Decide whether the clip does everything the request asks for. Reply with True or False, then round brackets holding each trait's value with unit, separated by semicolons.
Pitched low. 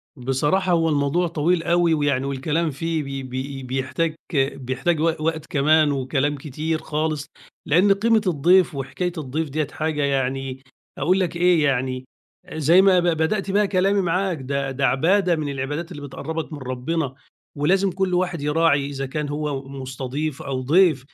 False (150 Hz)